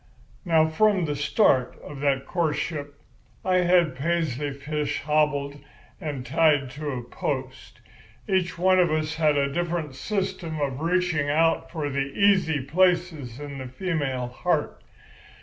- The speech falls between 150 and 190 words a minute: No, average, 140 wpm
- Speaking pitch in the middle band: Yes, medium, 150 Hz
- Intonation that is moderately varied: Yes, average, 3.6 semitones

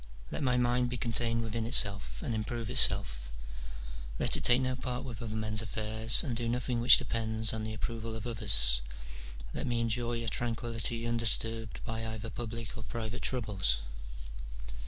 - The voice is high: No, low, 115 Hz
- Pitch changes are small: Yes, narrow, 1.6 semitones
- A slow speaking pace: No, average, 165 wpm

